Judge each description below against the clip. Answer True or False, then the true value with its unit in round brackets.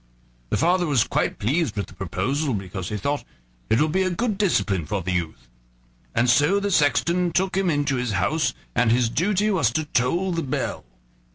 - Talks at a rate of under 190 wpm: False (195 wpm)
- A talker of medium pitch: True (145 Hz)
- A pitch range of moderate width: False (8.2 semitones)